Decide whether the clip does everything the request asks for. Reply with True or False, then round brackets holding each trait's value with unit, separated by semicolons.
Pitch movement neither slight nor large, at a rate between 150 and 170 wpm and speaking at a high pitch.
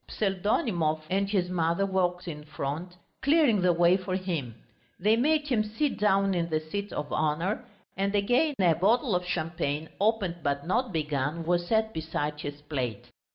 False (4.7 semitones; 165 wpm; 180 Hz)